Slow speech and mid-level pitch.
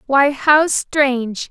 No: slow, 120 wpm; very high, 275 Hz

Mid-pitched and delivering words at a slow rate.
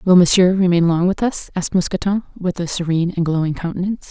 No: medium, 180 Hz; fast, 205 wpm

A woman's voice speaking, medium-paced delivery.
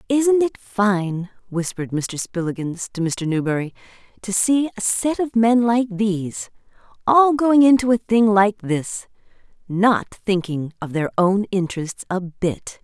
Yes: female; average, 150 wpm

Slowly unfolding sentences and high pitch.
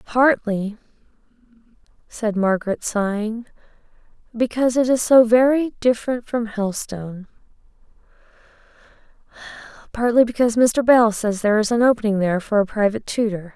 Yes: slow, 110 wpm; high, 225 Hz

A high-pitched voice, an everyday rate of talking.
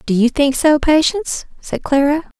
Yes: very high, 290 Hz; average, 175 wpm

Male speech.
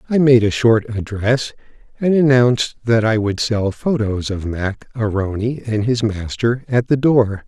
Yes: male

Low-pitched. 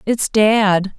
No: high, 205 Hz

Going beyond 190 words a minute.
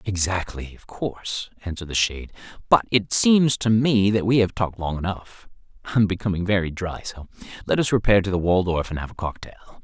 Yes: average, 200 wpm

